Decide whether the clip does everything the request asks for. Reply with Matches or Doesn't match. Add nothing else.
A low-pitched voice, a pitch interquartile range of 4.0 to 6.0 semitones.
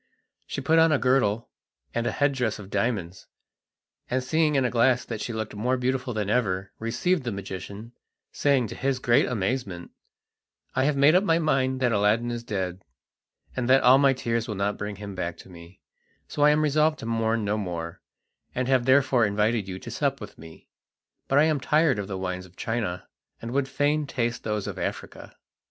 Matches